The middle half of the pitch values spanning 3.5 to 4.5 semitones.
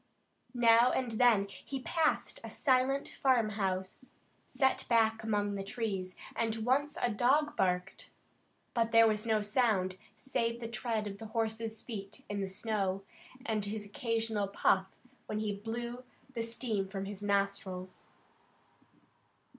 No: average, 3.0 semitones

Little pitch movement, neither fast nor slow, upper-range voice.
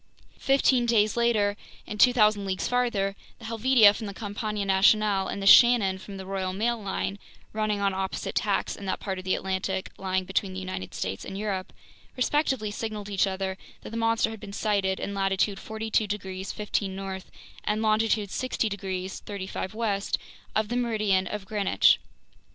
Yes: narrow, 2.3 semitones; average, 175 wpm; high, 205 Hz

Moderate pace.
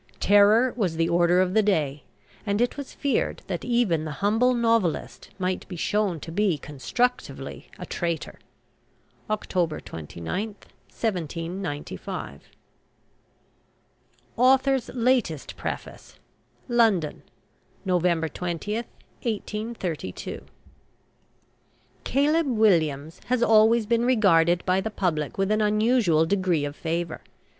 No: slow, 105 wpm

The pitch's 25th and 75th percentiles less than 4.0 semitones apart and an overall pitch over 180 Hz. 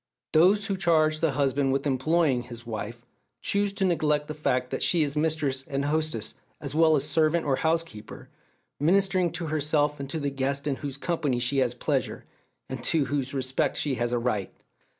No: average, 3.4 semitones; medium, 145 Hz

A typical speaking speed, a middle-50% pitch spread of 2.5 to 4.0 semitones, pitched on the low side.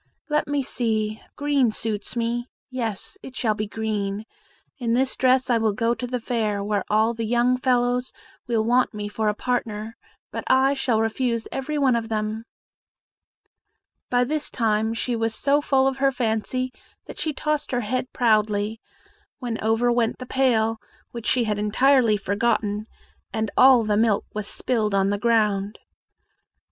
No: average, 165 wpm; average, 2.8 semitones; high, 230 Hz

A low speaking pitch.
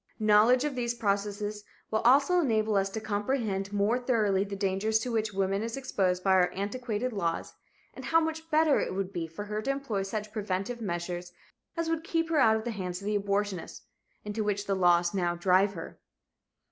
No: high, 210 Hz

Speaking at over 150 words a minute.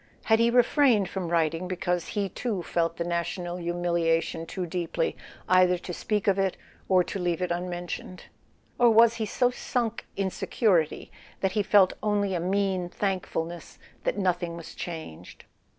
Yes: average, 160 wpm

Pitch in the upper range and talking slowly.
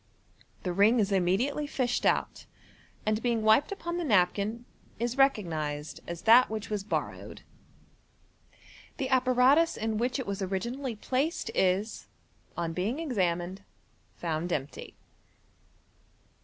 Yes: high, 220 Hz; slow, 120 wpm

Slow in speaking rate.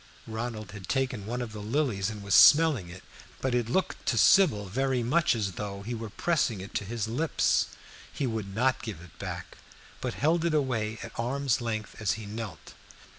No: average, 195 wpm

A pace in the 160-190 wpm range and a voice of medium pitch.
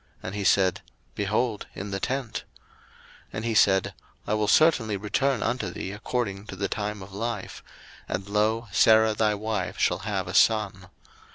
No: average, 170 wpm; low, 105 Hz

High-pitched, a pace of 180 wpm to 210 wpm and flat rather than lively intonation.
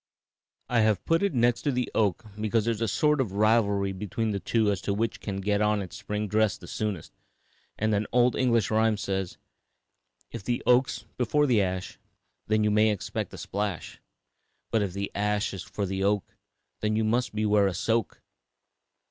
No: low, 105 Hz; average, 190 wpm; narrow, 2.3 semitones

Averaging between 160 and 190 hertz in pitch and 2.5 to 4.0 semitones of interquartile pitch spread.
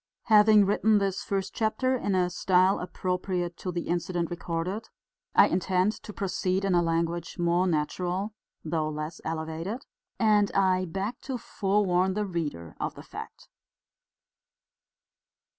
Yes: medium, 185 Hz; average, 2.8 semitones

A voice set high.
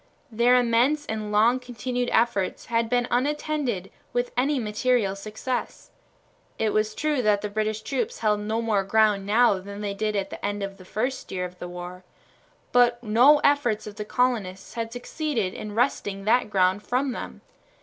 Yes: high, 220 Hz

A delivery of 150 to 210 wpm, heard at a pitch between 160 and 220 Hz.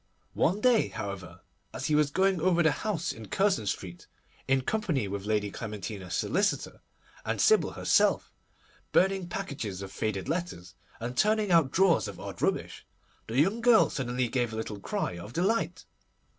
No: average, 160 wpm; medium, 140 Hz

